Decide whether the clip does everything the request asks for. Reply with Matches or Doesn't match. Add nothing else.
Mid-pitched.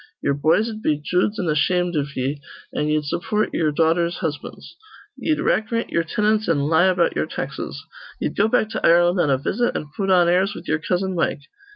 Matches